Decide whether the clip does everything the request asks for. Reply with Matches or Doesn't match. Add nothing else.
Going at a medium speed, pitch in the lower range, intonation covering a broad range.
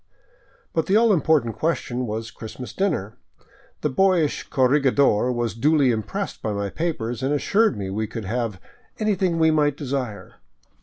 Matches